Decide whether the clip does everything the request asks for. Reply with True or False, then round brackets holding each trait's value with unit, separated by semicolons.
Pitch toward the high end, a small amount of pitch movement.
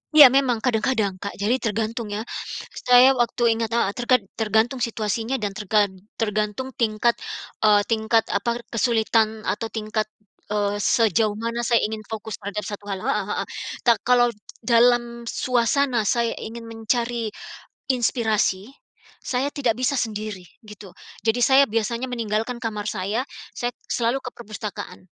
True (225 Hz; 2.3 semitones)